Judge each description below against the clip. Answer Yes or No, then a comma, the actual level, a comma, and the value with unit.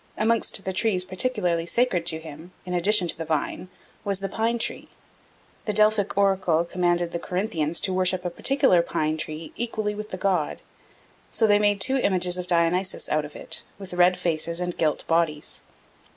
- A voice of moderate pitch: Yes, medium, 180 Hz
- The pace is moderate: Yes, average, 180 wpm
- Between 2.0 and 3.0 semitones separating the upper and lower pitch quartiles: No, average, 3.4 semitones